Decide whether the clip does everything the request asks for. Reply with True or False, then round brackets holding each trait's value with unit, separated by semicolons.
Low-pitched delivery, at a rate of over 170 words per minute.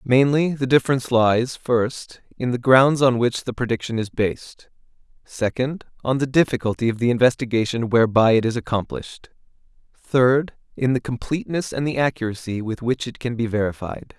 False (125 Hz; 160 wpm)